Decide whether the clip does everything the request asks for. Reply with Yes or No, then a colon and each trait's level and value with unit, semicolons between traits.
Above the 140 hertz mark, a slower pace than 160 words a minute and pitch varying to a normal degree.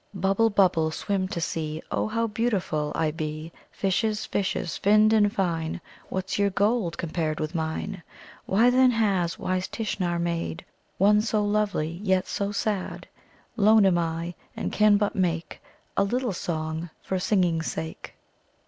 Yes: high, 190 Hz; average, 150 wpm; average, 4.0 semitones